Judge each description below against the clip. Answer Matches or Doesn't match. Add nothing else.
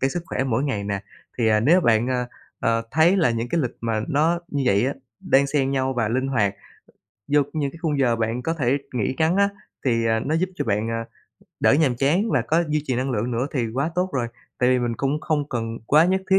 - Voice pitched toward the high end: Doesn't match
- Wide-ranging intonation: Doesn't match